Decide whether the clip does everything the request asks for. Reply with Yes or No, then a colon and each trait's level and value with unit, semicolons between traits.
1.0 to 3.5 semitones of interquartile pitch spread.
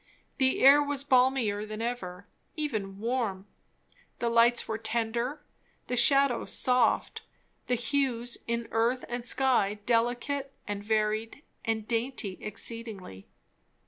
Yes: average, 2.9 semitones